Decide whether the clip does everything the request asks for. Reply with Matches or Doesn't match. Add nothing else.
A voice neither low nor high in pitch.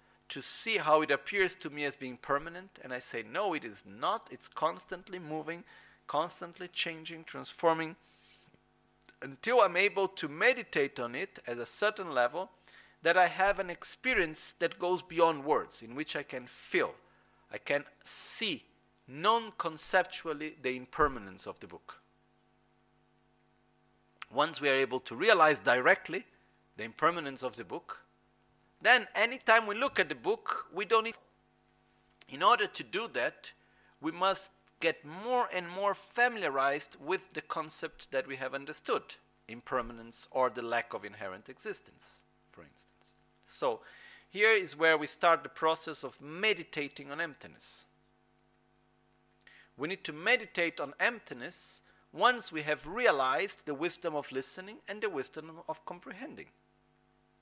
Matches